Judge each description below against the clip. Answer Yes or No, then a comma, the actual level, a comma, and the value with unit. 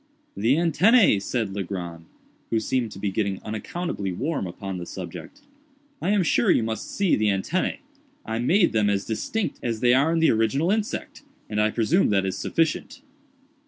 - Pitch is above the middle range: No, low, 115 Hz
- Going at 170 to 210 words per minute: Yes, average, 175 wpm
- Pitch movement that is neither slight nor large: No, wide, 8.8 semitones